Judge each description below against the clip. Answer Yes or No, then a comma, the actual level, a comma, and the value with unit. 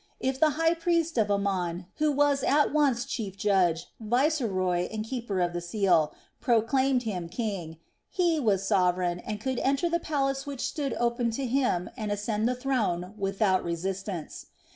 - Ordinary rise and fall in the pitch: No, wide, 6.4 semitones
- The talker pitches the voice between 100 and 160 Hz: No, high, 220 Hz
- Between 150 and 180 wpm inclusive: Yes, average, 165 wpm